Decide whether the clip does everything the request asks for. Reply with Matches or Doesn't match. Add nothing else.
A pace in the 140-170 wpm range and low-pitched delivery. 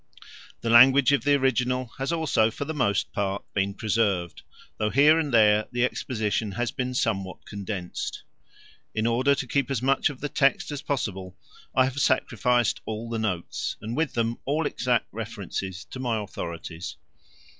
Matches